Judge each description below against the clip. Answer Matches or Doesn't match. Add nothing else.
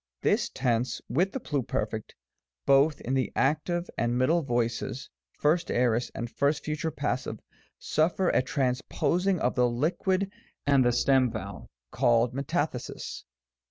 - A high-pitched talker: Doesn't match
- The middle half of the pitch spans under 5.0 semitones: Matches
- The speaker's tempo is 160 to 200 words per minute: Doesn't match